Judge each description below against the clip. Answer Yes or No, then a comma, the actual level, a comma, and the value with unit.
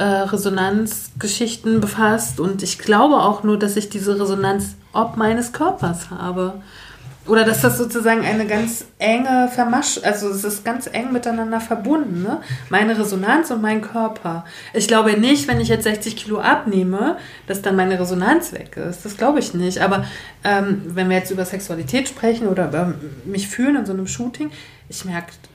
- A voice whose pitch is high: Yes, high, 210 Hz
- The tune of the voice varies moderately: Yes, average, 3.2 semitones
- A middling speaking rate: Yes, average, 170 wpm